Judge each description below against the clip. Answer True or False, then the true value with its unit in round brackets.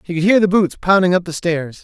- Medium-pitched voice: True (180 Hz)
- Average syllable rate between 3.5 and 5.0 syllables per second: False (5.9 syllables/s)